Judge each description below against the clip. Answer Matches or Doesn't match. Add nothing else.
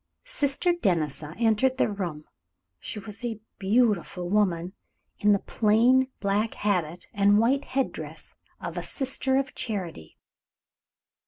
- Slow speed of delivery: Matches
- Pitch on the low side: Doesn't match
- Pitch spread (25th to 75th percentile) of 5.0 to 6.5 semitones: Matches